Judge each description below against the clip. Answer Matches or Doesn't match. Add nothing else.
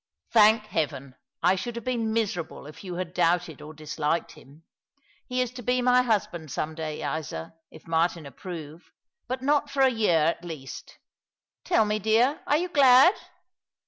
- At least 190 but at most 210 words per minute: Doesn't match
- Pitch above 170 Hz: Matches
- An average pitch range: Doesn't match